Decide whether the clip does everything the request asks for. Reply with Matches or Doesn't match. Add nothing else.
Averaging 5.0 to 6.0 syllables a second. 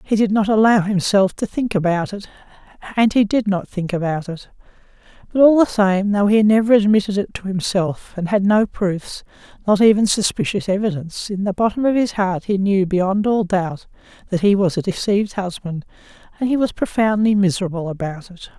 Matches